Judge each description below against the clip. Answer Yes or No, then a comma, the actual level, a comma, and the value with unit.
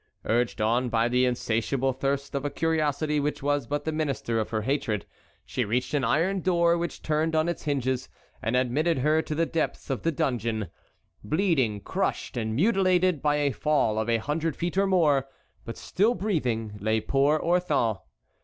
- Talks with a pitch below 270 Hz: Yes, medium, 140 Hz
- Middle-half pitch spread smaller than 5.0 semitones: No, average, 5.3 semitones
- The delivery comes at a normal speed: Yes, average, 180 wpm